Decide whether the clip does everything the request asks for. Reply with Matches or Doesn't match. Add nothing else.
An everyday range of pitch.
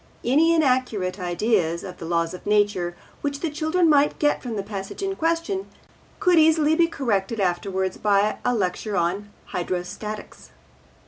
Doesn't match